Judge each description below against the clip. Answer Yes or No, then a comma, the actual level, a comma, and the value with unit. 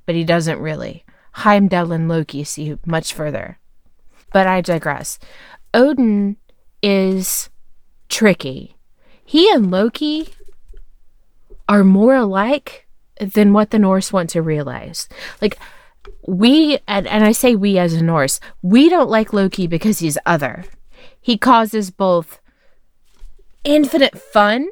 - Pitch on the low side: No, high, 200 Hz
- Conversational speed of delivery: No, slow, 125 wpm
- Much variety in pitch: Yes, wide, 6.5 semitones